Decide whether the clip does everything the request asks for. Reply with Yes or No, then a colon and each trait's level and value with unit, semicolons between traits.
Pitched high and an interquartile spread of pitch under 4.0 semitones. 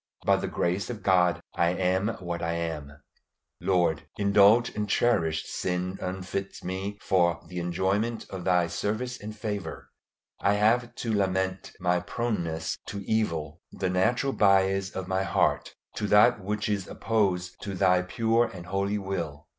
No: very low, 95 Hz; average, 2.8 semitones